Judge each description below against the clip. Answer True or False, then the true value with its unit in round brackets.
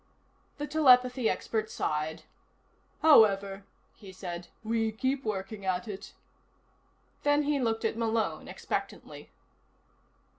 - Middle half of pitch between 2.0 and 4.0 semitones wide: False (4.5 semitones)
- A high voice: True (220 Hz)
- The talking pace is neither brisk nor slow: False (105 wpm)